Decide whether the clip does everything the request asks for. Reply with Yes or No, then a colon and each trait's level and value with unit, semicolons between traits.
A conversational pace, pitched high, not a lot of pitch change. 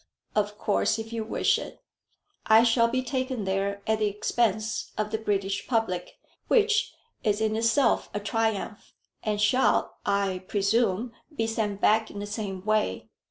Yes: average, 160 wpm; high, 215 Hz; narrow, 2.0 semitones